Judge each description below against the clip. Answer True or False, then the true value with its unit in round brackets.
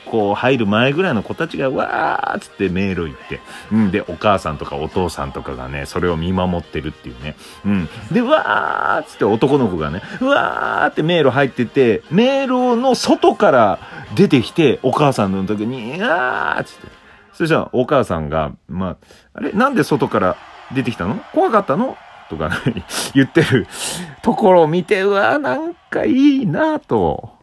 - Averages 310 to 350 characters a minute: True (340 characters per minute)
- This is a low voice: True (130 Hz)